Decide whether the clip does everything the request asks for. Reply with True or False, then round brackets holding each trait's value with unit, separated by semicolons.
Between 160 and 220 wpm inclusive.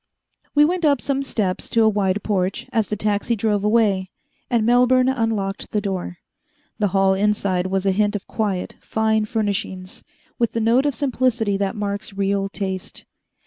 True (170 wpm)